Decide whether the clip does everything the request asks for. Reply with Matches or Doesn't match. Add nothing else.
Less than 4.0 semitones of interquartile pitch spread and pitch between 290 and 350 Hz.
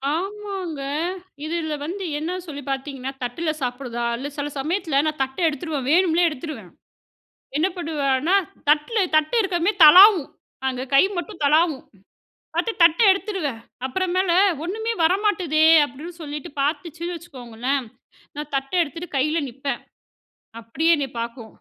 Doesn't match